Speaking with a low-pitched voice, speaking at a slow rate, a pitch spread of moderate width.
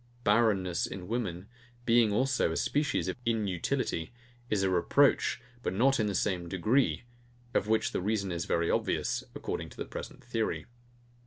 No: low, 105 Hz; average, 160 wpm; average, 4.4 semitones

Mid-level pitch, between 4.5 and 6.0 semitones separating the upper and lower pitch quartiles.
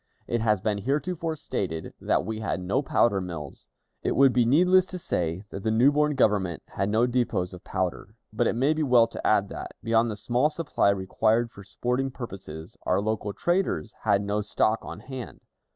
No: low, 110 Hz; average, 5.1 semitones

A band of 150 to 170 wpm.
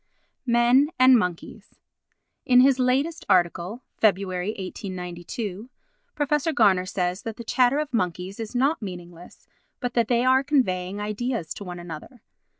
No: average, 140 wpm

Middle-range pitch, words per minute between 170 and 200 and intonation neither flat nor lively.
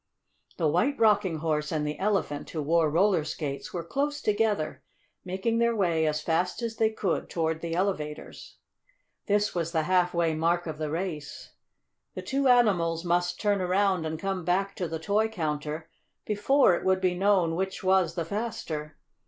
Yes: medium, 175 Hz; average, 175 wpm; average, 4.1 semitones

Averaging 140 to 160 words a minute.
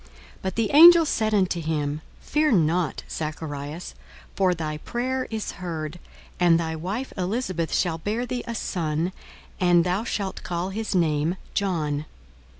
Yes: average, 150 wpm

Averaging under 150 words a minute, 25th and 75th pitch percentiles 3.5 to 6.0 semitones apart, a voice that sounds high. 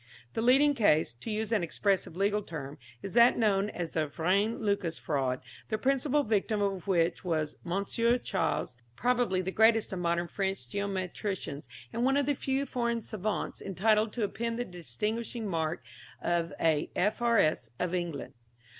No: average, 160 wpm; average, 5.2 semitones; high, 200 Hz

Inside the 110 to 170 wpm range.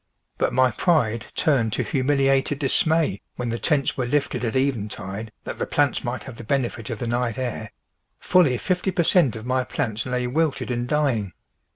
No: average, 185 wpm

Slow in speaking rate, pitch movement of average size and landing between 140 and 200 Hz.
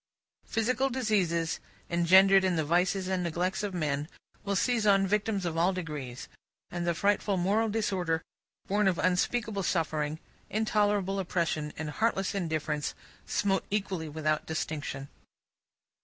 Yes: slow, 130 wpm; average, 3.9 semitones; medium, 185 Hz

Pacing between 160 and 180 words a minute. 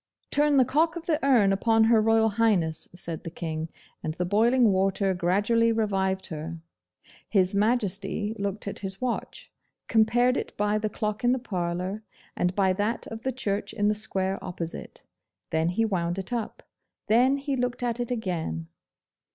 Yes: average, 170 wpm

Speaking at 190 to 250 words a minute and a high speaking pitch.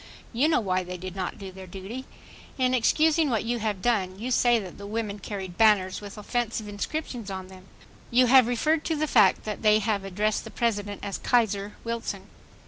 Yes: average, 195 wpm; high, 215 Hz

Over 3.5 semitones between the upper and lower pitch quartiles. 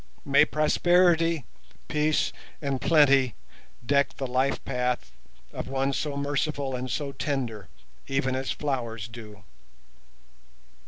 No: average, 2.8 semitones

